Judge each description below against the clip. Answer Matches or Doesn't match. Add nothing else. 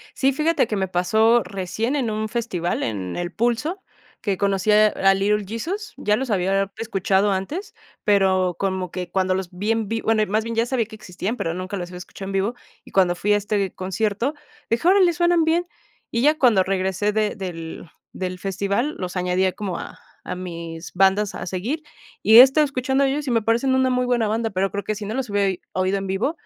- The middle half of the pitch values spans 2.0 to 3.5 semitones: Doesn't match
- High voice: Matches